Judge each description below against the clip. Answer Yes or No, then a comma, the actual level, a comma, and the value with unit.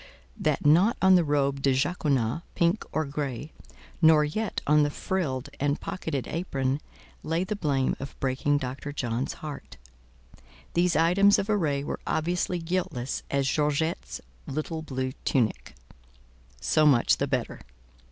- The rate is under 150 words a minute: Yes, average, 140 wpm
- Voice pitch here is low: No, medium, 150 Hz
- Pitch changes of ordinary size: Yes, average, 3.7 semitones